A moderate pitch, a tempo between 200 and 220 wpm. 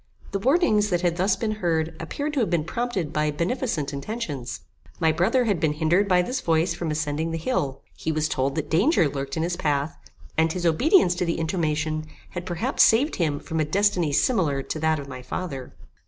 Yes: medium, 165 Hz; fast, 205 wpm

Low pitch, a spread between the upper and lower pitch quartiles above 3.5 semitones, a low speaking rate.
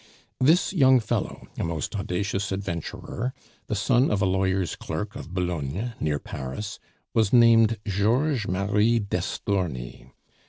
Yes: low, 100 Hz; average, 4.3 semitones; slow, 125 wpm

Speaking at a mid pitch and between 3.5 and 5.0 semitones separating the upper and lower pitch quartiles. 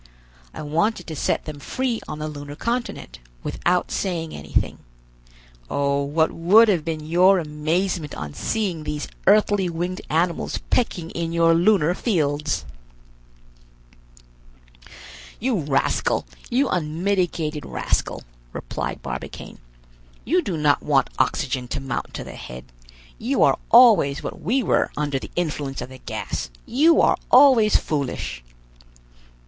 No: medium, 165 Hz; wide, 5.4 semitones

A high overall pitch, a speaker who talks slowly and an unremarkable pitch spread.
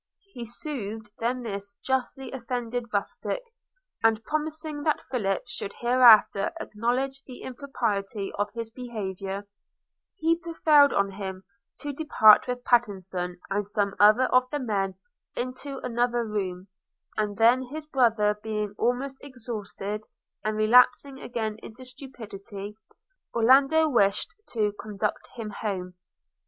Yes: high, 230 Hz; slow, 120 wpm; average, 4.0 semitones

